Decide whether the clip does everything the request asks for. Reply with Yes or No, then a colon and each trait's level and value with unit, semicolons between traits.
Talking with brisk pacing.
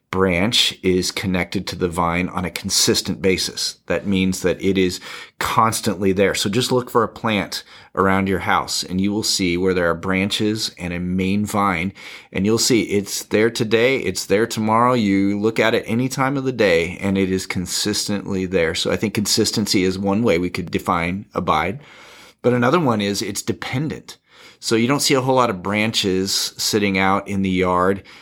No: average, 195 wpm